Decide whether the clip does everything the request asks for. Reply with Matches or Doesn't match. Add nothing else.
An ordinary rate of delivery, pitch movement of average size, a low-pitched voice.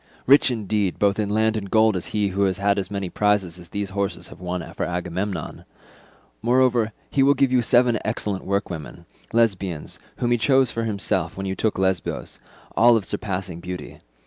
Matches